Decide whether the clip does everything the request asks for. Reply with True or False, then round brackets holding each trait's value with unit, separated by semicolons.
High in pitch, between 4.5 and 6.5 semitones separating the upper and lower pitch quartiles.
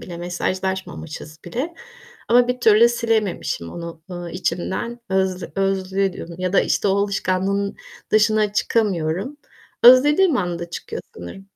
False (195 Hz; 3.9 semitones)